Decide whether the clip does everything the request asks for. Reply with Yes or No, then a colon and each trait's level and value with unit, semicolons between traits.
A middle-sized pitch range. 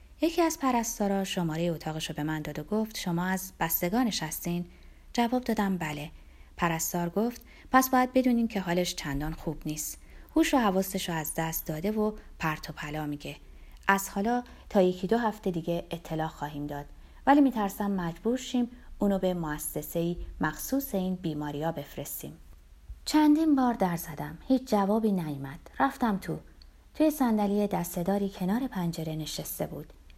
No: wide, 5.9 semitones